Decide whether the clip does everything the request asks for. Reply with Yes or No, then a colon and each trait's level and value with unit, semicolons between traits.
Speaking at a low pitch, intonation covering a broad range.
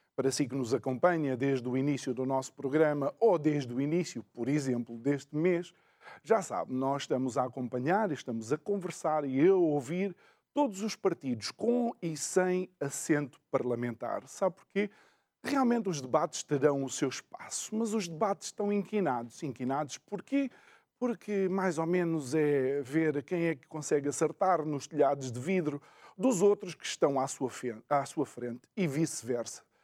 No: medium, 155 Hz; wide, 6.0 semitones